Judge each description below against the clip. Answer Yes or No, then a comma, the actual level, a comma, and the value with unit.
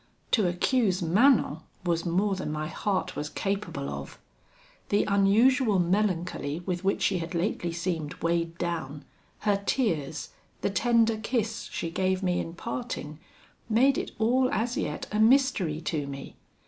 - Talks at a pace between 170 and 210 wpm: No, average, 150 wpm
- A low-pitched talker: No, medium, 185 Hz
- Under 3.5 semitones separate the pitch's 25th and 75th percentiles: No, average, 4.7 semitones